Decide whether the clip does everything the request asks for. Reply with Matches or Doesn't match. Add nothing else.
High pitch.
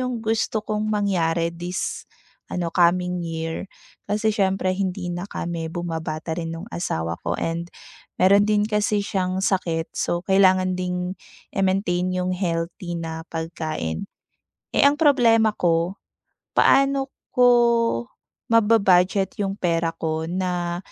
Doesn't match